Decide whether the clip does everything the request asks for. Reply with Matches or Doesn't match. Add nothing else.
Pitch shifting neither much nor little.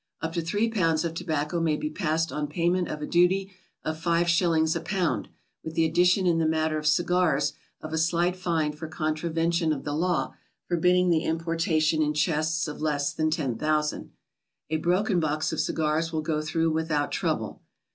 Doesn't match